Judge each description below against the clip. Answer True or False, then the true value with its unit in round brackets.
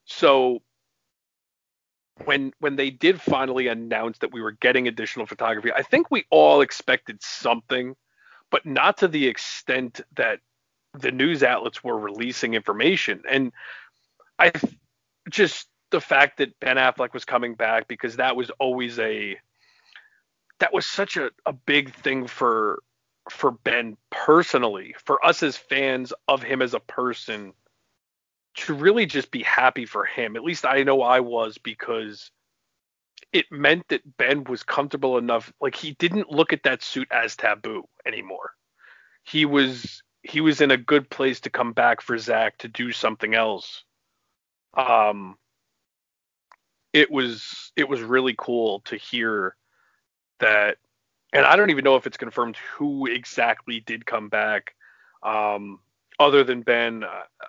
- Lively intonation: False (3.4 semitones)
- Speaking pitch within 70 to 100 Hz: False (125 Hz)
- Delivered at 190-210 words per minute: False (150 wpm)